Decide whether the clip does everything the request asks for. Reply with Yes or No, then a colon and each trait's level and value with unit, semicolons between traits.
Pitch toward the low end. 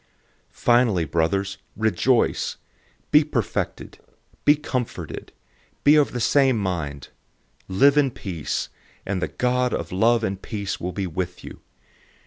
Yes: low, 105 Hz